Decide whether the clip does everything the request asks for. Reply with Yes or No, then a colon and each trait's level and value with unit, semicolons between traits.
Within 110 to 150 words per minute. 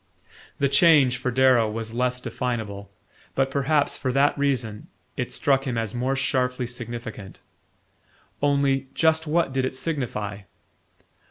Yes: slow, 135 wpm